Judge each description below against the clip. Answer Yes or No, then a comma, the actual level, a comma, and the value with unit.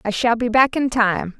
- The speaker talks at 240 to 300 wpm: Yes, fast, 260 wpm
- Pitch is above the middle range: Yes, high, 230 Hz